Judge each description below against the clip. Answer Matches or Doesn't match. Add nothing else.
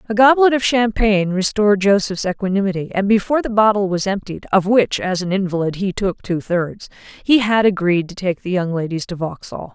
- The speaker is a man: Doesn't match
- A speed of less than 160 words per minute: Doesn't match